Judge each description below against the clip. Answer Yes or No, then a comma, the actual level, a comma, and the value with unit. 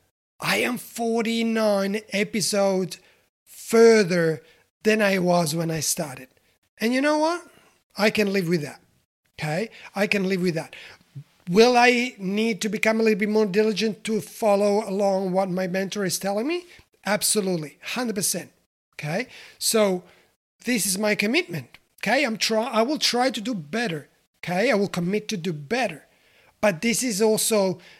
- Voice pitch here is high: Yes, high, 205 Hz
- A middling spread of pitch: Yes, average, 3.3 semitones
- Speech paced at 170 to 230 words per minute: No, average, 155 wpm